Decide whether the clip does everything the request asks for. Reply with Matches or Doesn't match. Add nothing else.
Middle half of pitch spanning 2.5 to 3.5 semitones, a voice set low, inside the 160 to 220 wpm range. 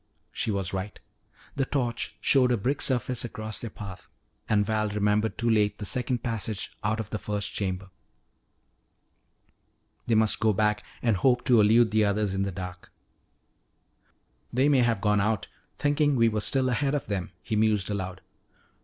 Matches